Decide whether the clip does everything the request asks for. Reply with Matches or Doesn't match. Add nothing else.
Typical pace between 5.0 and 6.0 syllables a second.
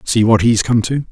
Matches